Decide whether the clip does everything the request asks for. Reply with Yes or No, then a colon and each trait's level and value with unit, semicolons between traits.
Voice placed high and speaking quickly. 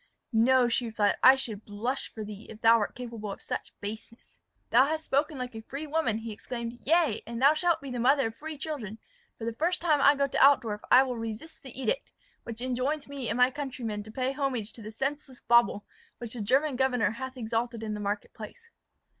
Yes: high, 245 Hz; fast, 220 wpm